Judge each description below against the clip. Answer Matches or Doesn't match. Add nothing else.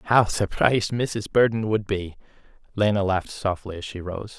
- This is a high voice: Doesn't match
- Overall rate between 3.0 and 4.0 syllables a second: Doesn't match